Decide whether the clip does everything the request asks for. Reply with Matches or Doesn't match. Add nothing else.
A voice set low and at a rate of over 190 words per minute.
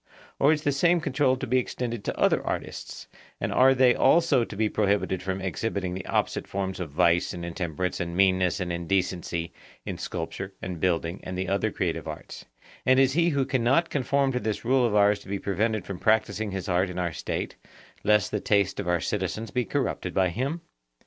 Matches